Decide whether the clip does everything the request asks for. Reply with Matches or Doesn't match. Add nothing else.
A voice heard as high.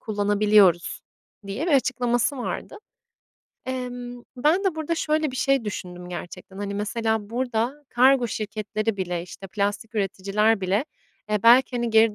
Matches